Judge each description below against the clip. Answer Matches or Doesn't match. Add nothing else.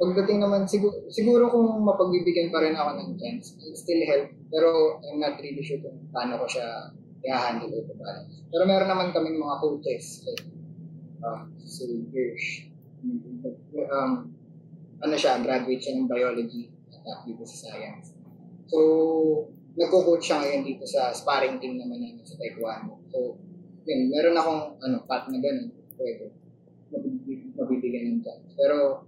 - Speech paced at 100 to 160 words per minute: Matches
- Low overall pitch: Doesn't match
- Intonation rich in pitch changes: Matches